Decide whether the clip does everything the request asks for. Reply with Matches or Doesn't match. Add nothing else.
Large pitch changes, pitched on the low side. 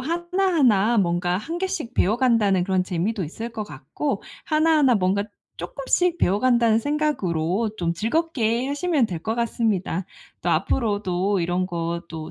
Doesn't match